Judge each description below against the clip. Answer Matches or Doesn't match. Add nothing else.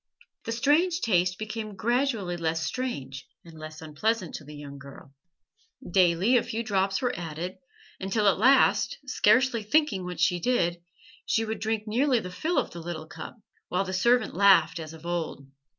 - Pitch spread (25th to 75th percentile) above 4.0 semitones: Matches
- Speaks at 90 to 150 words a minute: Doesn't match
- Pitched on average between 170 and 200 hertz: Matches